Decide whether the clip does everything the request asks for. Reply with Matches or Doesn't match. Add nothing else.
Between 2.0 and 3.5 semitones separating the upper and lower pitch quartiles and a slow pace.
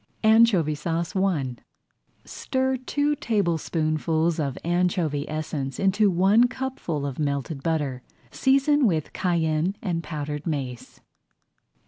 Doesn't match